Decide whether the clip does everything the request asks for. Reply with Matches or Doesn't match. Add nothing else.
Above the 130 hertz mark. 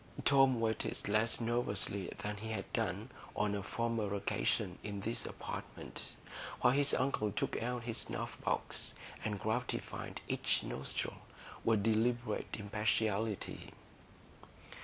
Doesn't match